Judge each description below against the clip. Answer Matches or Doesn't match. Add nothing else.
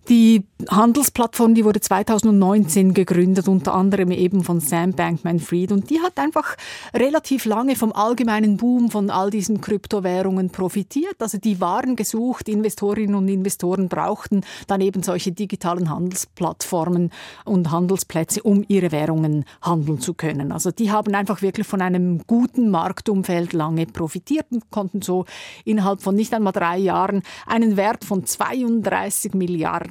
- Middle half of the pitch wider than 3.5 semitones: Doesn't match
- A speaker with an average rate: Matches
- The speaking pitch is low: Doesn't match